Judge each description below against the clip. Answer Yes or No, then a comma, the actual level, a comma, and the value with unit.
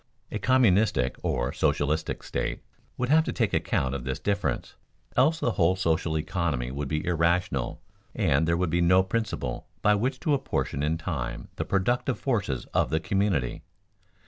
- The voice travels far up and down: Yes, wide, 6.4 semitones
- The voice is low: Yes, very low, 85 Hz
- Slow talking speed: No, average, 165 wpm